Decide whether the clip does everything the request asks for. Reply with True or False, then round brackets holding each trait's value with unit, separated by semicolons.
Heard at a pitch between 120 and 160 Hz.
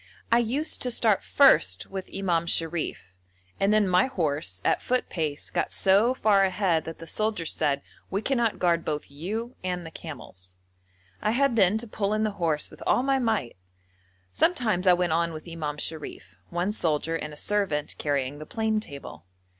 False (180 Hz)